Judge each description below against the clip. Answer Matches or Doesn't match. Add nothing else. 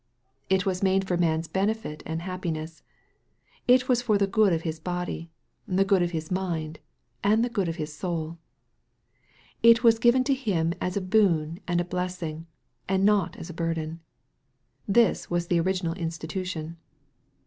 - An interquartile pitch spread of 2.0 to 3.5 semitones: Matches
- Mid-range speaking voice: Matches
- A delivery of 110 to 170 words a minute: Matches